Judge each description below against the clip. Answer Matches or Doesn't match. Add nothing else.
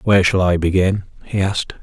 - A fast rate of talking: Doesn't match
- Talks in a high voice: Doesn't match